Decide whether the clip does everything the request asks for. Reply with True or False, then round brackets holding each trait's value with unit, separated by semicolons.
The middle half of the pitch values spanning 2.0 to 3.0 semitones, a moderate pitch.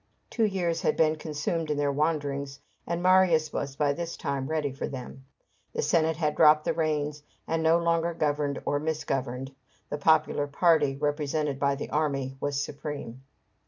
True (2.4 semitones; 150 Hz)